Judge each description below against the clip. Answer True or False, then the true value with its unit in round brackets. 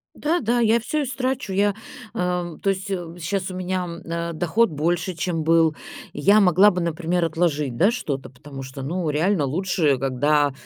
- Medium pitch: True (175 Hz)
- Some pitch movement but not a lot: True (4.0 semitones)